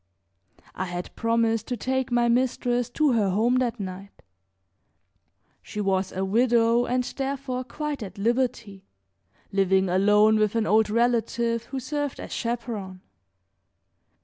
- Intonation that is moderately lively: Yes, average, 3.5 semitones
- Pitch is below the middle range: No, high, 230 Hz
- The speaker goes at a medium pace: No, slow, 130 wpm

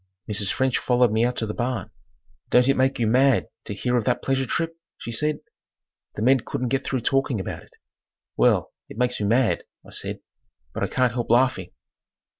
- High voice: No, low, 125 Hz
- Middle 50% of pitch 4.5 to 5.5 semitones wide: No, average, 2.7 semitones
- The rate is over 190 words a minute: Yes, average, 200 wpm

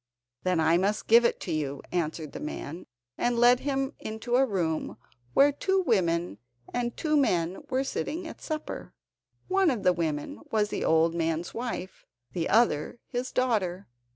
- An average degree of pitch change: No, wide, 7.2 semitones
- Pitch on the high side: Yes, high, 210 Hz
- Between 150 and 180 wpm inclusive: Yes, average, 165 wpm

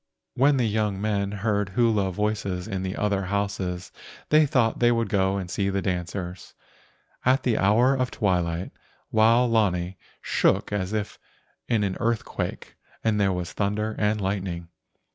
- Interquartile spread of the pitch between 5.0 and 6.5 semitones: No, average, 2.9 semitones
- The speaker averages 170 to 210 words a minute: No, average, 155 wpm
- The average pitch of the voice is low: Yes, low, 100 Hz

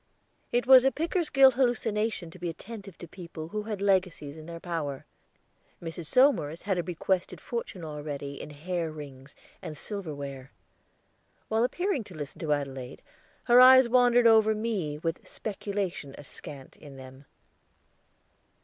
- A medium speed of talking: Yes, average, 145 wpm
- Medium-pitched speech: Yes, medium, 175 Hz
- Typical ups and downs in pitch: No, wide, 7.1 semitones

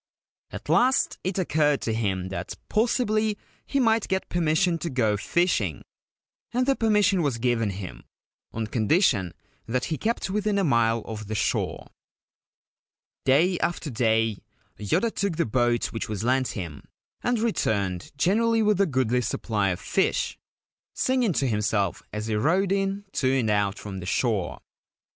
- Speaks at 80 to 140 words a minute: No, average, 155 wpm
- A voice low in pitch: Yes, low, 130 Hz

